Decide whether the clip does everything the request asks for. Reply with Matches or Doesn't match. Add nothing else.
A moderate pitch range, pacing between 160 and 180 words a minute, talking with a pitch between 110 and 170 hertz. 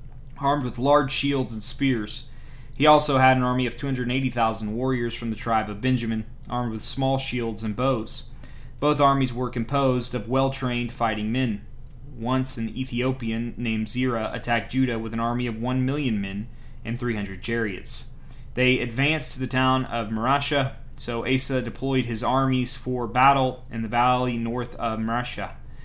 Doesn't match